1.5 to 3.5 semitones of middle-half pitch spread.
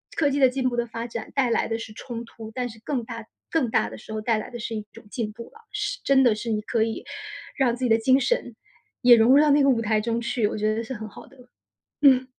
Yes: average, 2.8 semitones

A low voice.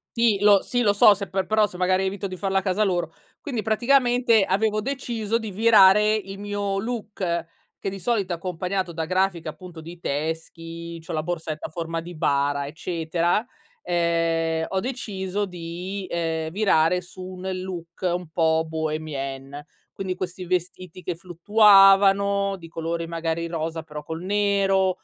No: medium, 185 Hz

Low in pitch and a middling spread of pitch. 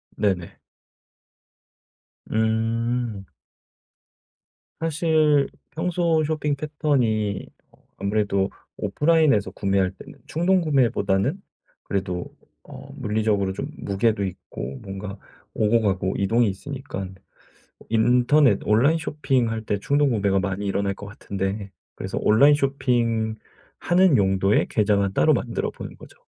No: low, 110 Hz; wide, 6.2 semitones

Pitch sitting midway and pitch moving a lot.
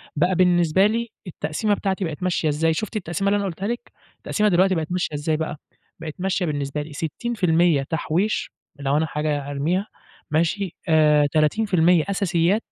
No: medium, 170 Hz; average, 4.0 semitones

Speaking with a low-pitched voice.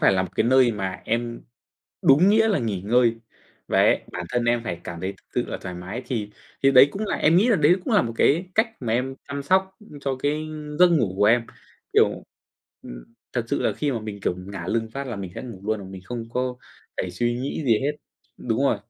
Yes: low, 120 Hz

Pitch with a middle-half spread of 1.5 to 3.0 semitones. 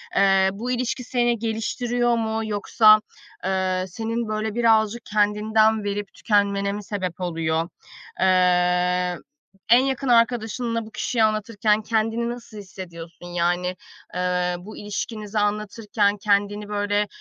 Yes: narrow, 2.6 semitones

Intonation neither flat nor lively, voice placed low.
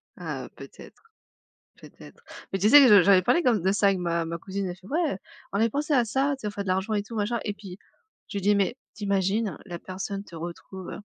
No: average, 3.2 semitones; high, 200 Hz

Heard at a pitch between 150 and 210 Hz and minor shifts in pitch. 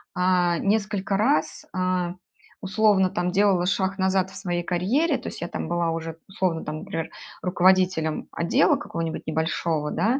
Yes: medium, 185 Hz; narrow, 2.3 semitones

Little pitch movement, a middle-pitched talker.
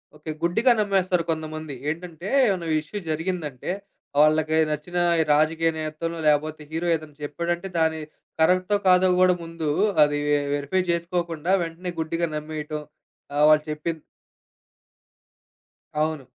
Yes: narrow, 2.2 semitones; medium, 160 Hz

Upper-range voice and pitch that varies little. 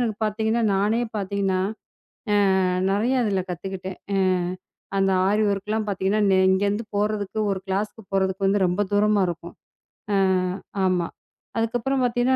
Yes: high, 200 Hz; narrow, 2.1 semitones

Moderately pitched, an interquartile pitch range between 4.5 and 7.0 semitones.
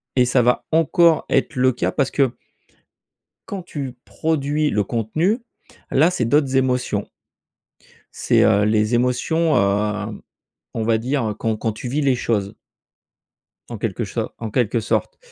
No: low, 125 Hz; average, 4.8 semitones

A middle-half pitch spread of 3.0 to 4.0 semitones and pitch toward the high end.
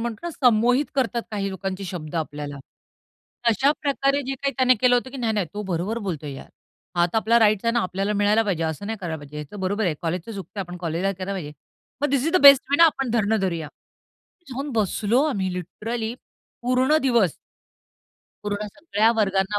No: average, 5.1 semitones; high, 210 Hz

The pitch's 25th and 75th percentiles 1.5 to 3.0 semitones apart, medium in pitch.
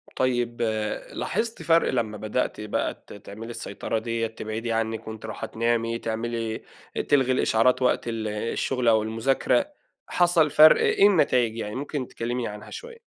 No: average, 2.7 semitones; low, 115 Hz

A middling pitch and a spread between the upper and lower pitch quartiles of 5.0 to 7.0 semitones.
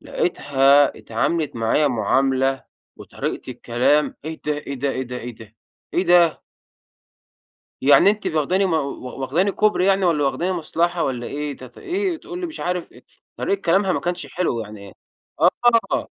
Yes: medium, 150 Hz; average, 5.3 semitones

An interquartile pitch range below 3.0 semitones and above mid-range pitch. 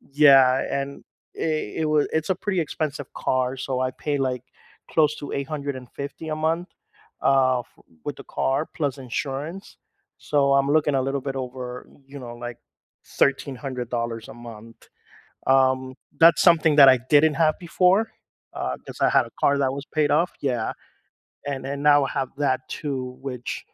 No: narrow, 2.6 semitones; medium, 140 Hz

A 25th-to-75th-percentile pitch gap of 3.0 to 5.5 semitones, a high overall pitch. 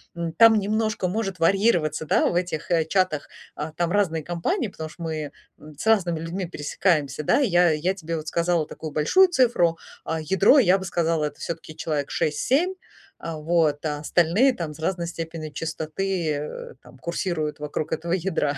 No: average, 3.5 semitones; medium, 170 Hz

